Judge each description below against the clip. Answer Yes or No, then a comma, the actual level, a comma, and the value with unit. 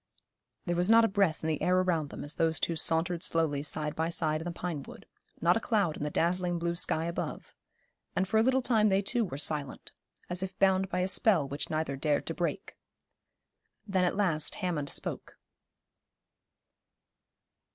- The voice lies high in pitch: No, medium, 170 Hz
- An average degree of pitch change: Yes, average, 3.4 semitones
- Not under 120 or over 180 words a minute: No, average, 190 wpm